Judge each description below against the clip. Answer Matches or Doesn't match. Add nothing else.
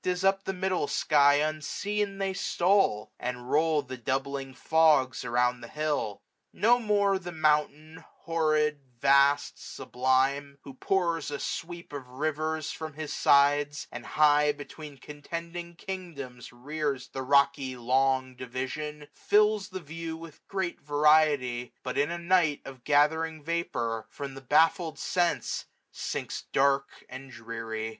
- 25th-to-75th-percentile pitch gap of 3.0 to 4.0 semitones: Matches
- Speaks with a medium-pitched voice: Matches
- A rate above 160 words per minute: Doesn't match